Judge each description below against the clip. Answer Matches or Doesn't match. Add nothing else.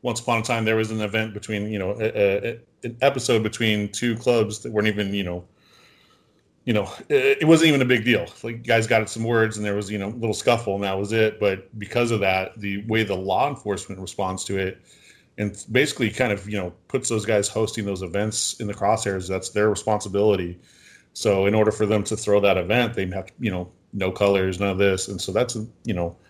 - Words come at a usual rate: Doesn't match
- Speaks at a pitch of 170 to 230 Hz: Doesn't match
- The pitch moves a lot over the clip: Doesn't match